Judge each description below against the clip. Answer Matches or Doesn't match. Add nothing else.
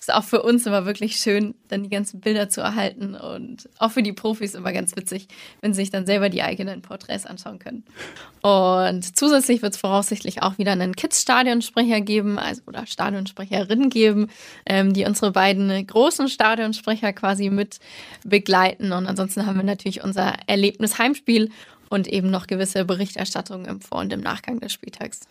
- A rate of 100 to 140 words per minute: Doesn't match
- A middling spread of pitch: Doesn't match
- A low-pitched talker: Doesn't match